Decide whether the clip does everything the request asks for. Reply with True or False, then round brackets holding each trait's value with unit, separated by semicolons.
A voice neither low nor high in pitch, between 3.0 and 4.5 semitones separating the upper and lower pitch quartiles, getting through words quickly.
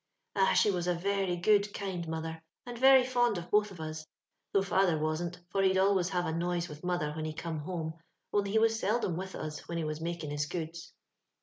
True (175 Hz; 3.6 semitones; 225 wpm)